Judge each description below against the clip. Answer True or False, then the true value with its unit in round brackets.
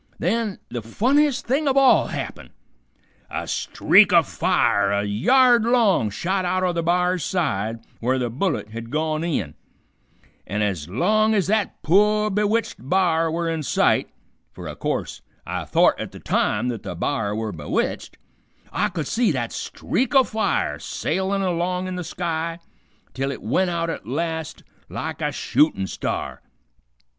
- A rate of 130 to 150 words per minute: False (160 wpm)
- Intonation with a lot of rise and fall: True (8.2 semitones)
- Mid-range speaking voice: True (170 Hz)